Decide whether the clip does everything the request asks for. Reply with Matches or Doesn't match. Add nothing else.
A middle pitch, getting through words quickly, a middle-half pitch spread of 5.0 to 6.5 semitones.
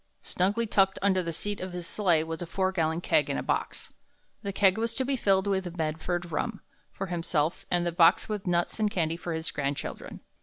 Doesn't match